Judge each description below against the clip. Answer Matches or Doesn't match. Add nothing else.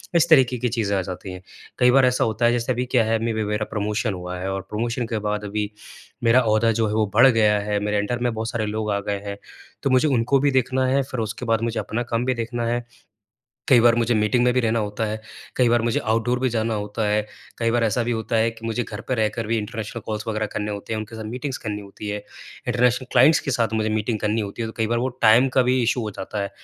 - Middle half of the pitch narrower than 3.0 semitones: Matches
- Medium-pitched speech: Doesn't match